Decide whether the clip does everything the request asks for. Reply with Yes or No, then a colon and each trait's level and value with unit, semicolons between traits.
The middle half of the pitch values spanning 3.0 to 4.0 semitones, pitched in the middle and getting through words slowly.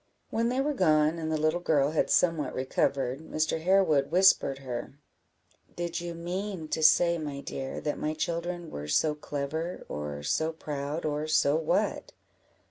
No: average, 3.3 semitones; medium, 155 Hz; average, 160 wpm